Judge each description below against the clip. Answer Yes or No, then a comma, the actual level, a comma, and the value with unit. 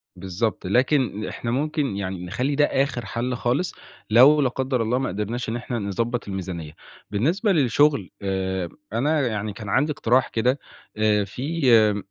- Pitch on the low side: Yes, low, 120 Hz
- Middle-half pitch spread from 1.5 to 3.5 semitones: No, average, 4.9 semitones